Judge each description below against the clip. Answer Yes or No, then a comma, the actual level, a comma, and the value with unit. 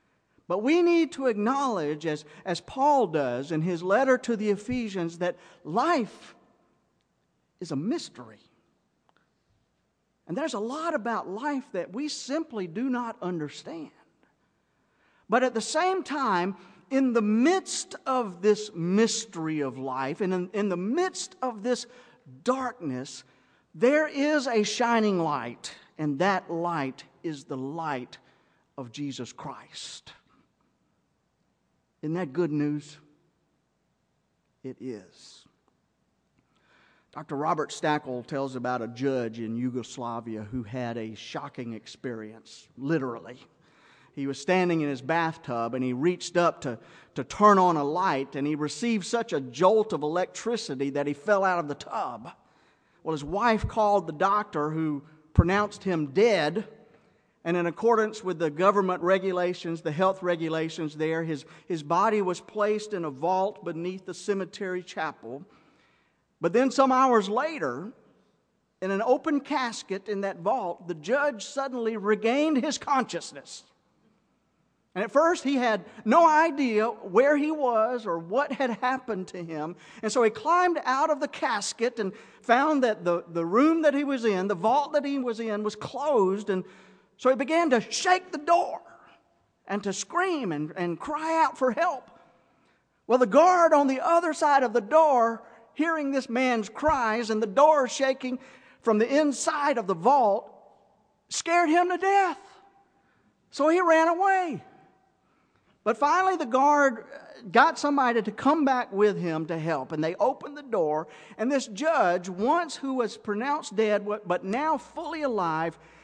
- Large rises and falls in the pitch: Yes, wide, 8.2 semitones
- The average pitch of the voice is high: Yes, high, 215 Hz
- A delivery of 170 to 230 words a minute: No, average, 150 wpm